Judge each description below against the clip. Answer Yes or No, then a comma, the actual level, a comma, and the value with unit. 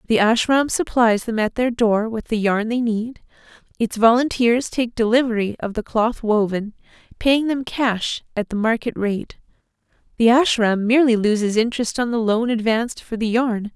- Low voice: No, high, 230 Hz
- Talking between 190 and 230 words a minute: No, average, 170 wpm